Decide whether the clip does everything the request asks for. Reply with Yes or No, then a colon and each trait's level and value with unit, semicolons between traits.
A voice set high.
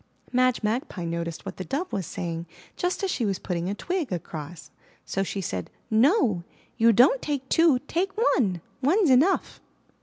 Yes: high, 225 Hz